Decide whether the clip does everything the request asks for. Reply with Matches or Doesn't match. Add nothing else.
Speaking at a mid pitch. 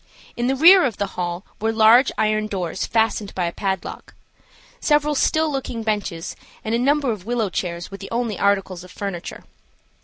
Doesn't match